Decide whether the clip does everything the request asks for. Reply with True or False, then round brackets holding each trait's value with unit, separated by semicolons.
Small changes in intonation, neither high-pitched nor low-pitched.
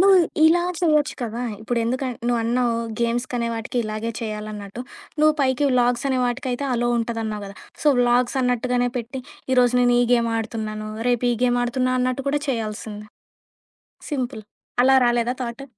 False (2.0 semitones; 245 Hz)